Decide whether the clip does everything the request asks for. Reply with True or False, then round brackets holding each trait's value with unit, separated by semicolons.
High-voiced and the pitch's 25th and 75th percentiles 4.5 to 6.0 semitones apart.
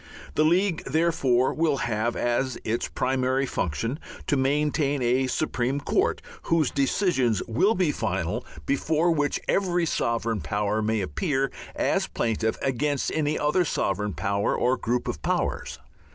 False (135 Hz; 4.9 semitones)